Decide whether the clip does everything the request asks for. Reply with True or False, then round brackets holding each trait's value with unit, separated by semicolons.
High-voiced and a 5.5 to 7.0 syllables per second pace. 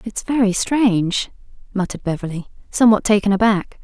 True (205 Hz; 5.8 syllables/s)